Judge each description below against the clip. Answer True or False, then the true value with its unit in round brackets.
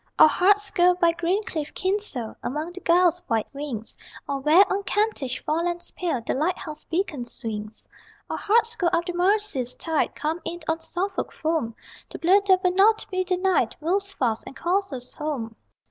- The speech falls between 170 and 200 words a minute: True (180 wpm)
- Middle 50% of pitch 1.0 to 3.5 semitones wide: False (4.7 semitones)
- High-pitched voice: True (340 Hz)